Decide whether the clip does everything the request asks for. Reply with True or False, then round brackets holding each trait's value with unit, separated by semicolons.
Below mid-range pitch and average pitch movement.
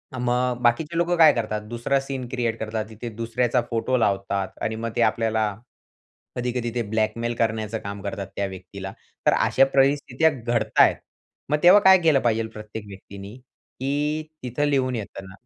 True (115 Hz; 3.4 semitones)